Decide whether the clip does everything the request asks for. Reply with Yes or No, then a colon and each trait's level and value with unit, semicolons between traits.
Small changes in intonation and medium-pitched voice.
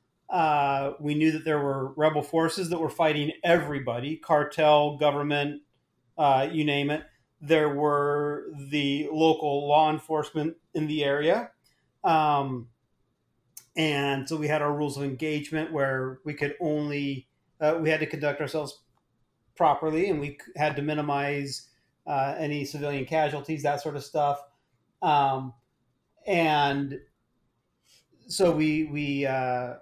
Yes: narrow, 1.7 semitones; medium, 145 Hz